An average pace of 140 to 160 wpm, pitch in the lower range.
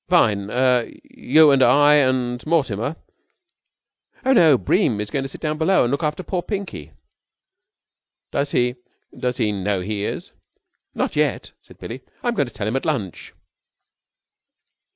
Yes: average, 155 wpm; low, 130 Hz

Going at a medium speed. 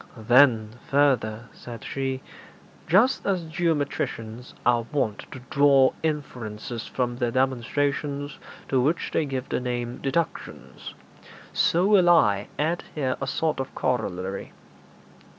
No: slow, 120 wpm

